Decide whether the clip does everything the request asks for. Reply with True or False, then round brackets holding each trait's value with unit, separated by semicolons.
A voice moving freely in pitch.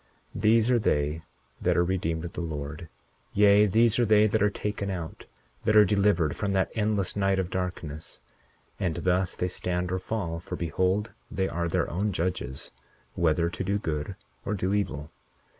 False (3.6 semitones)